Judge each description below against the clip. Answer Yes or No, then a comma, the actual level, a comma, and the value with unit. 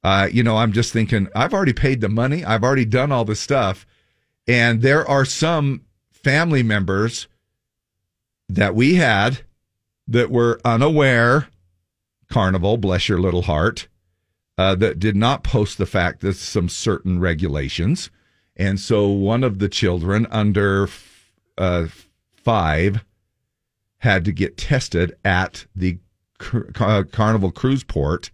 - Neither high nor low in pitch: No, low, 105 Hz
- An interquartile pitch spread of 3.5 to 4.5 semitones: Yes, average, 4.0 semitones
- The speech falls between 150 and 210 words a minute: No, average, 140 wpm